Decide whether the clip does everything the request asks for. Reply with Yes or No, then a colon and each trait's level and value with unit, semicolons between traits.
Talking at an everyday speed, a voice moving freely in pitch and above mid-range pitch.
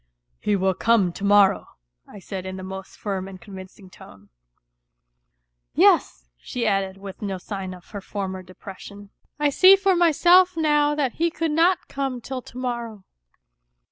Yes: average, 175 wpm; wide, 7.4 semitones; high, 205 Hz